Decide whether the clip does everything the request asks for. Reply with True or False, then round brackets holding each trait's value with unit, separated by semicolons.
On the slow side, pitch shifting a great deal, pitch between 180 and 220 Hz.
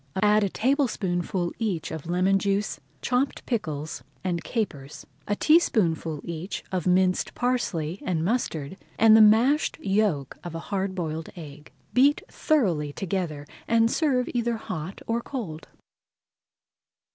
True (130 wpm; 5.7 semitones; 190 Hz)